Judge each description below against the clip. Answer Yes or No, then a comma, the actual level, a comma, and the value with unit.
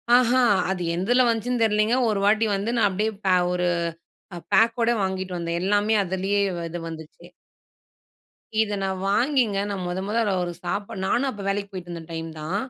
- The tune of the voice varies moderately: Yes, average, 3.5 semitones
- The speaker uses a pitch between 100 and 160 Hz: No, high, 200 Hz